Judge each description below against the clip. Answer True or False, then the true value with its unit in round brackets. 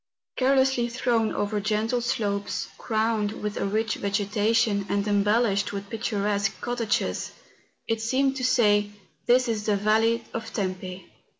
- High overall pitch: True (215 Hz)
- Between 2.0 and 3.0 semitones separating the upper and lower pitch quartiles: True (2.4 semitones)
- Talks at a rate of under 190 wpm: True (135 wpm)